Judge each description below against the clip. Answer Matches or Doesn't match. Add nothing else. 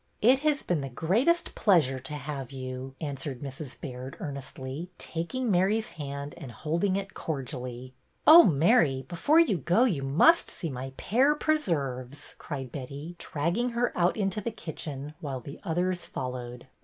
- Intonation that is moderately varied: Doesn't match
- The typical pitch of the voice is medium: Matches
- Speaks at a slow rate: Doesn't match